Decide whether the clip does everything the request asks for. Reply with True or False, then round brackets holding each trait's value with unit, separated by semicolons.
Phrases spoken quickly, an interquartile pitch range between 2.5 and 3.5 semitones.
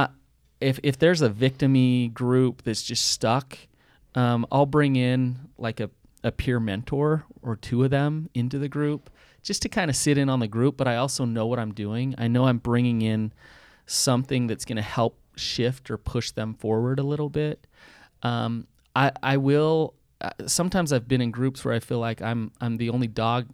False (195 wpm; 3.1 semitones)